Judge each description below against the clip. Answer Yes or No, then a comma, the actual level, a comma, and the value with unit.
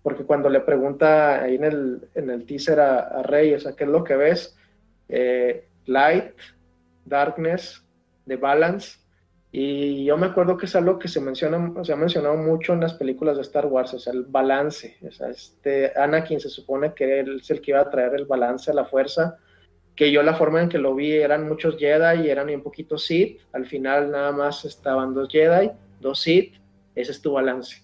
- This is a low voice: No, medium, 145 Hz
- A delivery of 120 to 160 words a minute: No, fast, 205 wpm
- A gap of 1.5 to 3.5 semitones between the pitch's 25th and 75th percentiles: Yes, average, 2.8 semitones